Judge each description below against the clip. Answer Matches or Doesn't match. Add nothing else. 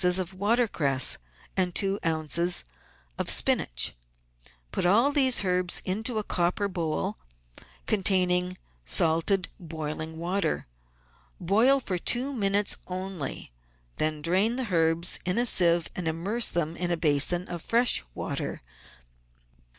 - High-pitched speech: Doesn't match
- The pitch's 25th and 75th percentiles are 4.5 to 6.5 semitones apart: Doesn't match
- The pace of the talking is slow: Matches